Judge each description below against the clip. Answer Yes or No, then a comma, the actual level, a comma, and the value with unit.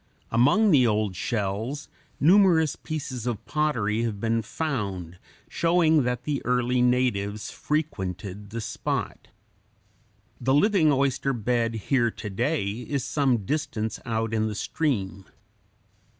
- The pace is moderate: No, slow, 120 wpm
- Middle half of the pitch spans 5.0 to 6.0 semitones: Yes, wide, 5.5 semitones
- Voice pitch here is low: Yes, low, 120 Hz